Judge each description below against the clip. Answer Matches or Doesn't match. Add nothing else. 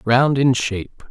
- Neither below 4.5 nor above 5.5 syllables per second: Doesn't match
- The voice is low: Matches